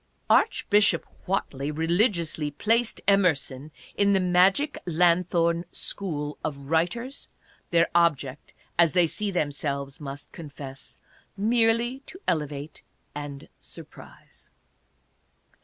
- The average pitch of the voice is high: No, medium, 170 Hz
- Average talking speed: No, slow, 105 wpm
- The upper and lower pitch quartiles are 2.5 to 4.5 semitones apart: No, wide, 5.4 semitones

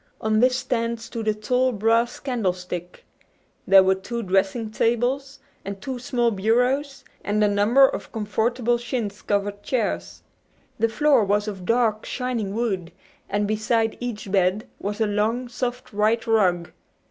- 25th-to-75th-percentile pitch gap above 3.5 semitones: No, average, 3.0 semitones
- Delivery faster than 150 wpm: No, average, 145 wpm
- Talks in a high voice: Yes, high, 220 Hz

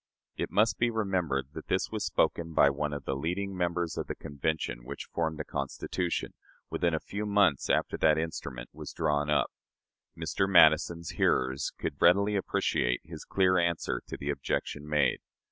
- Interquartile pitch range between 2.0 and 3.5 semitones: No, average, 4.2 semitones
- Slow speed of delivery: No, average, 175 wpm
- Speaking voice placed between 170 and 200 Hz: No, very low, 80 Hz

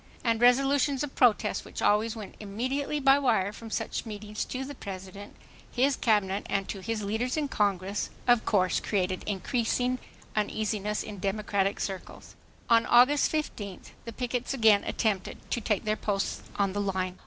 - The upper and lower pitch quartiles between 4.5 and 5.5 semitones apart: No, average, 3.7 semitones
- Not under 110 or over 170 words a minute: Yes, average, 160 wpm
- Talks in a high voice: Yes, high, 215 Hz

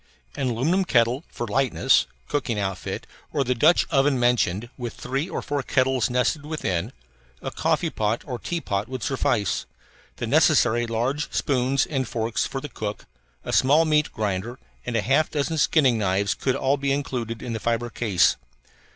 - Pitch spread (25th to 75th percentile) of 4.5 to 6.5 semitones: No, average, 3.8 semitones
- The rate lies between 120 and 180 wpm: Yes, average, 170 wpm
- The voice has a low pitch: Yes, low, 125 Hz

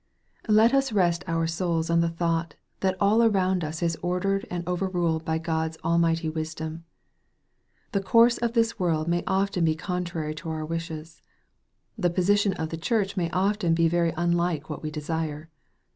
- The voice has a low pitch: No, medium, 170 Hz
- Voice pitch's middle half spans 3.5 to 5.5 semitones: No, average, 2.8 semitones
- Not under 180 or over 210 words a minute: No, average, 170 wpm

